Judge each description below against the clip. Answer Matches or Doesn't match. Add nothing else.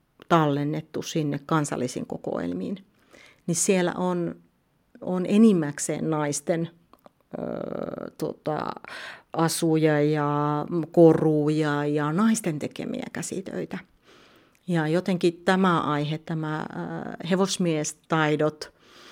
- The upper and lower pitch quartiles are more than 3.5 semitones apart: Doesn't match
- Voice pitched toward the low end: Doesn't match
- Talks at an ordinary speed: Doesn't match